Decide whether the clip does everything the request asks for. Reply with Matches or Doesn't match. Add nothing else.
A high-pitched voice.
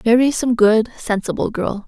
Matches